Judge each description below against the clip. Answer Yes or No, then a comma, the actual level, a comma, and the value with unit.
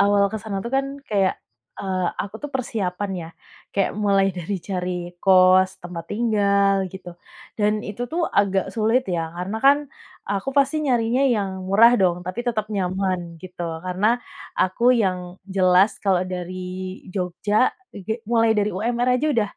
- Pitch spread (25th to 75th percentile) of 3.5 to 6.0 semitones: No, average, 3.1 semitones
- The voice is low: No, high, 200 Hz